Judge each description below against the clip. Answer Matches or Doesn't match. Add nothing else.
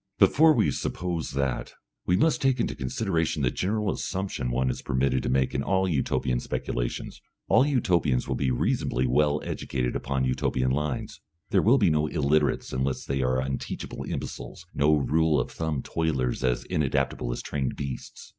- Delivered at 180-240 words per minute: Doesn't match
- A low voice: Matches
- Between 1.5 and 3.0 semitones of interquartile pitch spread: Doesn't match